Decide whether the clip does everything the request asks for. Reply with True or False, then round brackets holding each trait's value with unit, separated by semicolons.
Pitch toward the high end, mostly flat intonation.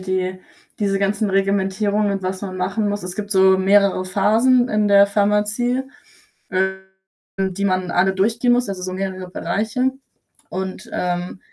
True (195 Hz; 1.9 semitones)